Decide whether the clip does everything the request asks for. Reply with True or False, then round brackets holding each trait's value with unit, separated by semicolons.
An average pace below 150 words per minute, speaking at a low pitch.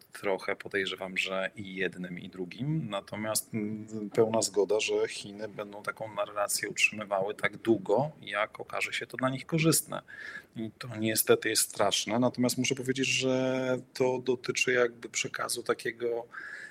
True (140 wpm; 120 Hz)